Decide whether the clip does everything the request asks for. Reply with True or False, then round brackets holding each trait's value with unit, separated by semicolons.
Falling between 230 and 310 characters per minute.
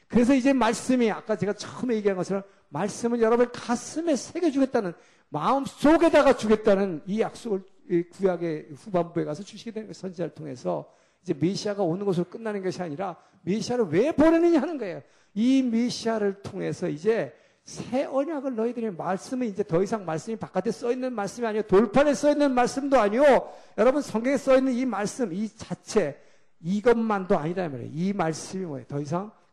False (390 characters per minute)